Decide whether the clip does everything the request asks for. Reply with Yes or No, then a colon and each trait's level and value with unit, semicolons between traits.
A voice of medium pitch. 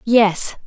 No: high, 215 Hz